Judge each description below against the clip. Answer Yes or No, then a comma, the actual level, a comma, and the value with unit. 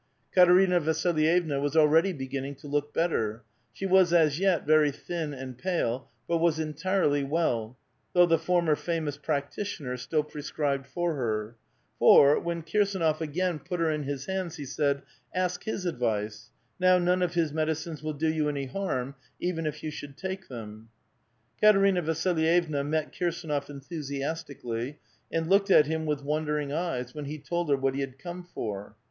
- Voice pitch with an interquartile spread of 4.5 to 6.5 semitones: No, average, 3.7 semitones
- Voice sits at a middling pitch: Yes, medium, 155 Hz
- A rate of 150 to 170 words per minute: Yes, average, 165 wpm